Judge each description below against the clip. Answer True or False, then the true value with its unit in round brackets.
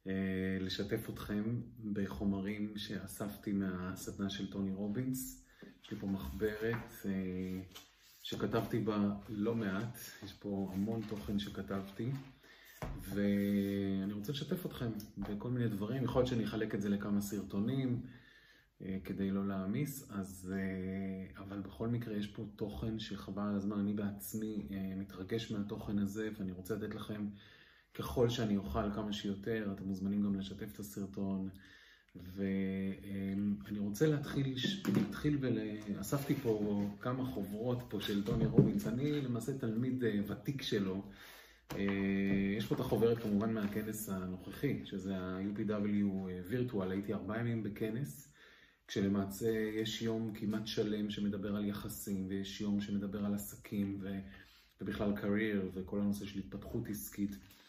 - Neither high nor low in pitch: False (100 Hz)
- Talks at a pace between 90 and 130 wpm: True (125 wpm)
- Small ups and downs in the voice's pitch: True (2.1 semitones)